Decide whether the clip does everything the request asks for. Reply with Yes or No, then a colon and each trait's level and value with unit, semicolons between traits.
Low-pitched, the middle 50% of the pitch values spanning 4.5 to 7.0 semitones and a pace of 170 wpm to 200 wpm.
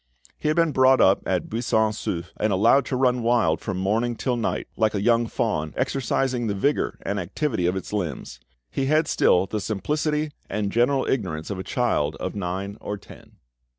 Yes: low, 110 Hz; average, 5.2 semitones; average, 190 wpm